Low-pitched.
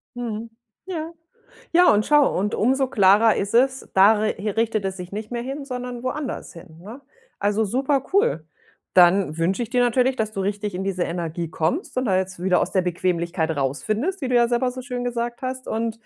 No: high, 220 Hz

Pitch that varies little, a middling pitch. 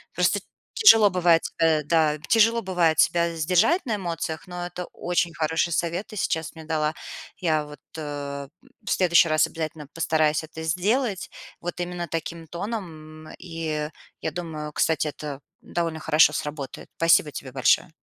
Yes: narrow, 2.3 semitones; medium, 165 Hz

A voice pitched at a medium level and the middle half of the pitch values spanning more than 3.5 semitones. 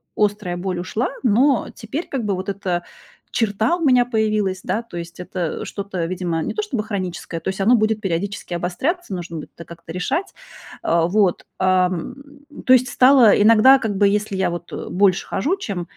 No: high, 200 Hz; average, 4.1 semitones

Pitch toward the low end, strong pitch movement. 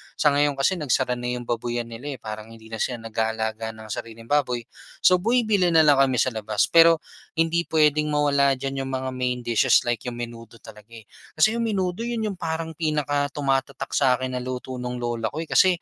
No: low, 130 Hz; average, 4.5 semitones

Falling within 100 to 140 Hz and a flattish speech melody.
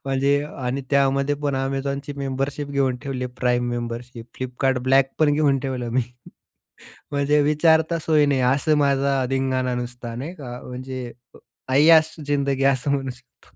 Yes: low, 135 Hz; narrow, 1.9 semitones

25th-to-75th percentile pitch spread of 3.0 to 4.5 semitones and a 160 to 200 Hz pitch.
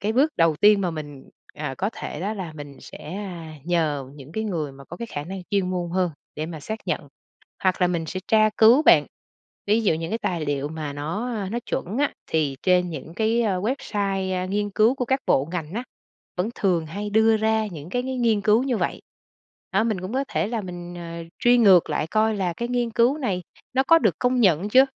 No: average, 5.0 semitones; high, 190 Hz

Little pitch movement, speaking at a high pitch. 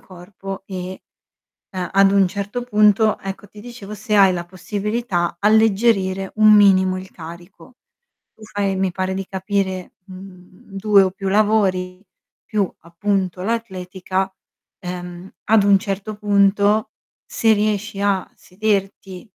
Yes: narrow, 2.0 semitones; high, 195 Hz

